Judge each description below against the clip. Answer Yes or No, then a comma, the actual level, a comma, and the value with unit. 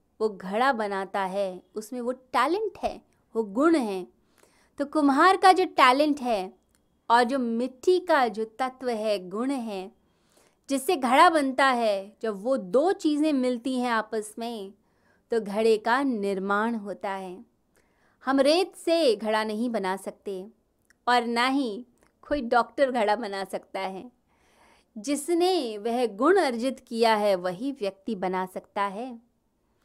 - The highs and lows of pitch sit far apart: No, average, 4.8 semitones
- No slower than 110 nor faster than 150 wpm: Yes, average, 145 wpm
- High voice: Yes, high, 235 Hz